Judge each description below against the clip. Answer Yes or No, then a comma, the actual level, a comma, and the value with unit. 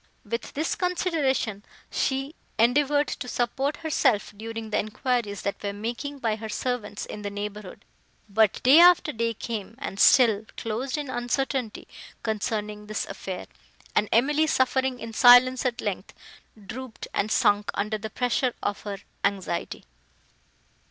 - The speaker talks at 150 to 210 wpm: No, average, 140 wpm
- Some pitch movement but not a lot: Yes, average, 3.9 semitones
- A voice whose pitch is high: Yes, high, 230 Hz